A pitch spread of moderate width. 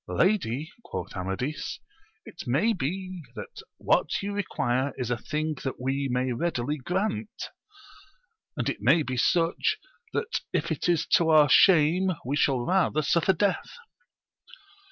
No: wide, 6.1 semitones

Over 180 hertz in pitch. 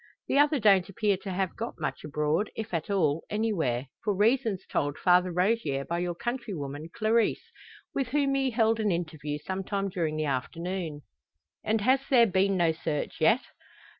Yes: high, 190 Hz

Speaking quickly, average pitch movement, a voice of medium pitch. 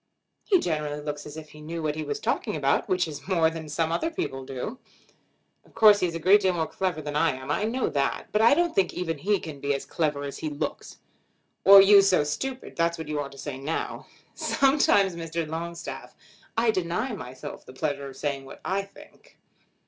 Yes: fast, 215 wpm; average, 4.8 semitones; medium, 165 Hz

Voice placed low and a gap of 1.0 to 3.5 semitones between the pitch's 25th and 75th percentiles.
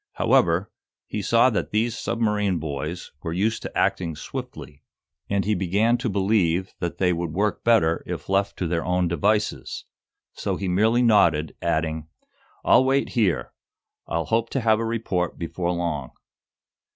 No: very low, 95 Hz; average, 4.5 semitones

